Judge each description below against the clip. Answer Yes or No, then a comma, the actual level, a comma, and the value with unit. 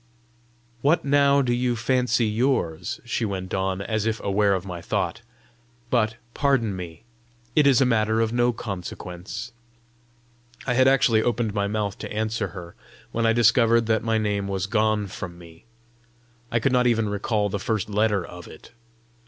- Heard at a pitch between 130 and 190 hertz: No, low, 110 Hz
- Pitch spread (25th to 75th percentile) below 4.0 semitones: Yes, average, 3.4 semitones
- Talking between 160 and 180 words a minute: Yes, average, 170 wpm